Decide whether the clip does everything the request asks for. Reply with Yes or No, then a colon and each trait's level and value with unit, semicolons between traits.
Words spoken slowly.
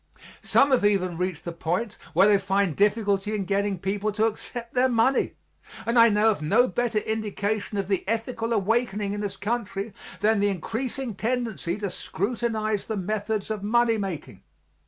No: average, 170 wpm